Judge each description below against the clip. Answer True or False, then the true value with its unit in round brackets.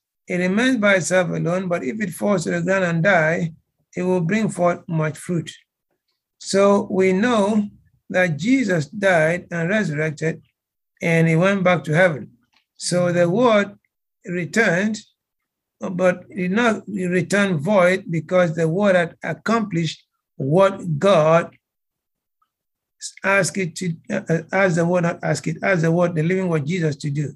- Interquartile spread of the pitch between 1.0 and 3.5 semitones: True (3.1 semitones)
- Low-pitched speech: False (180 Hz)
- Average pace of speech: True (150 wpm)